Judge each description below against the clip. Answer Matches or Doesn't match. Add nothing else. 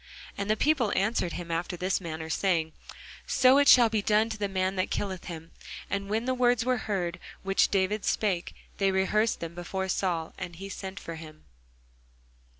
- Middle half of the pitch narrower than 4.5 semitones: Matches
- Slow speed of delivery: Doesn't match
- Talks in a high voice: Matches